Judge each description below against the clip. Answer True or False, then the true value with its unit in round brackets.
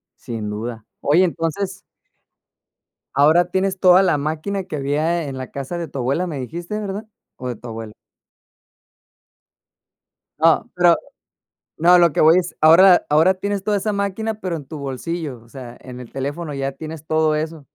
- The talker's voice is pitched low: False (160 Hz)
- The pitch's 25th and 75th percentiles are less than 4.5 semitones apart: False (4.9 semitones)